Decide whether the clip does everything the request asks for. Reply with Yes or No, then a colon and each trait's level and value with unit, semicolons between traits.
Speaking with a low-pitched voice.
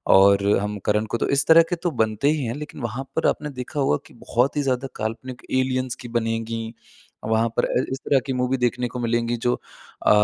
Yes: low, 125 Hz